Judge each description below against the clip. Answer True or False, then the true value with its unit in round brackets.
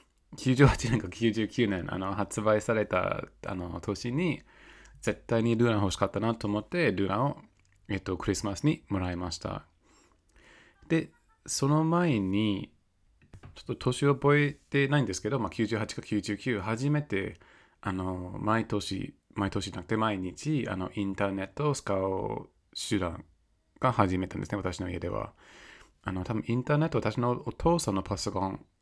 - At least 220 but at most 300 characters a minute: True (290 characters per minute)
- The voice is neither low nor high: False (105 Hz)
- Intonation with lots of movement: False (4.9 semitones)